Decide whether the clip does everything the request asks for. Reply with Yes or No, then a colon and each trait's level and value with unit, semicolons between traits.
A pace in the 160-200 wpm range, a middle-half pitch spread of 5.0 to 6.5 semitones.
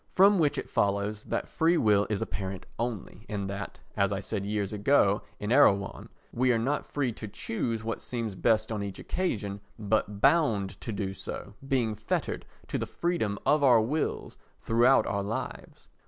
No: average, 175 wpm; average, 4.0 semitones